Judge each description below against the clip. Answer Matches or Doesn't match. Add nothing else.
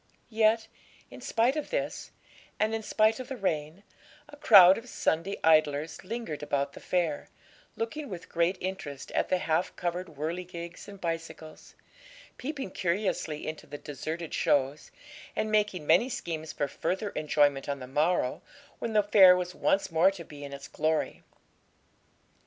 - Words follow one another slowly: Doesn't match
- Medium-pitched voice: Matches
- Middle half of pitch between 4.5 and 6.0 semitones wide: Matches